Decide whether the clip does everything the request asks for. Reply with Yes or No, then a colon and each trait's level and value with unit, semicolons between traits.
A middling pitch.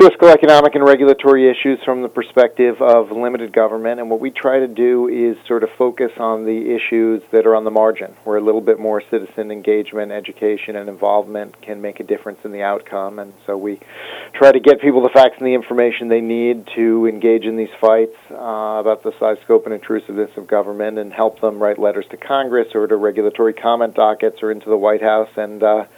No: low, 110 Hz